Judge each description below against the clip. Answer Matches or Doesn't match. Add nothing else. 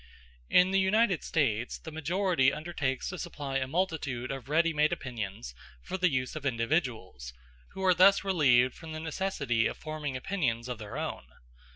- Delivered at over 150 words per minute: Matches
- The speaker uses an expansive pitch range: Matches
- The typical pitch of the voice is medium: Matches